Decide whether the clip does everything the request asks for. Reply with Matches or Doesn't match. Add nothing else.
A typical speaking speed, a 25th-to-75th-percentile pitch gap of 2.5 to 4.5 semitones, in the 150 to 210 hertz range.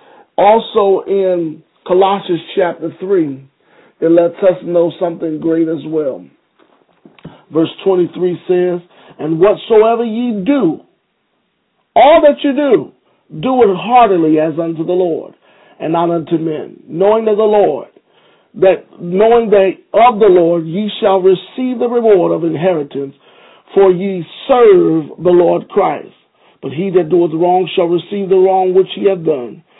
Matches